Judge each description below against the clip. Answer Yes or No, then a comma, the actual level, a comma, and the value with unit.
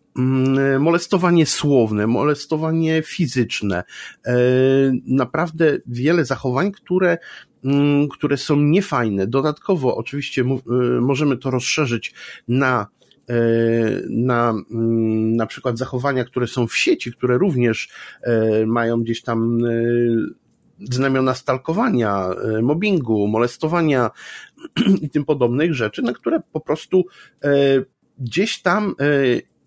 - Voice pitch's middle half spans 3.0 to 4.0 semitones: No, average, 4.6 semitones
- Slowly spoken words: Yes, slow, 90 wpm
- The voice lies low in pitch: Yes, low, 130 Hz